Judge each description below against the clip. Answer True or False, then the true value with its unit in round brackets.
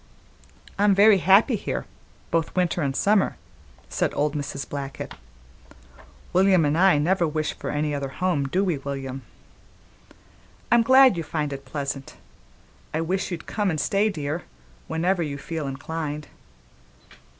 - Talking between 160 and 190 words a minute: False (140 wpm)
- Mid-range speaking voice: True (160 Hz)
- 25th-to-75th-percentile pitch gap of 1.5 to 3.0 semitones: False (4.8 semitones)